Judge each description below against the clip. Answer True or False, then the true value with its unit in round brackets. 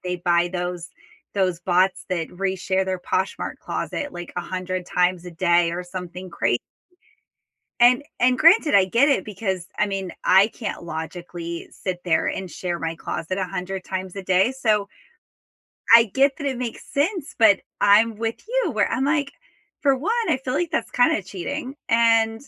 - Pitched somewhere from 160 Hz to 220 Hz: True (190 Hz)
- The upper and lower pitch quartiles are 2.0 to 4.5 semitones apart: False (5.5 semitones)